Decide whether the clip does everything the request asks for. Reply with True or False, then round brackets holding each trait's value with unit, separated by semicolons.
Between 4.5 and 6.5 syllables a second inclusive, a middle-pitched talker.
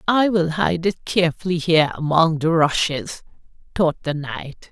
True (4.6 syllables/s; 165 Hz)